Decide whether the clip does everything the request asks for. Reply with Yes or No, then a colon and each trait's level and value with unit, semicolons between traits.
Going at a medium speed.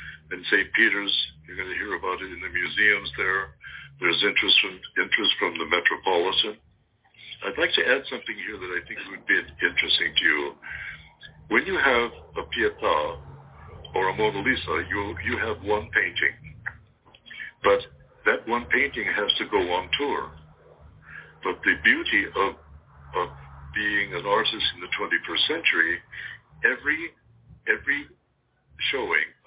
Yes: average, 145 wpm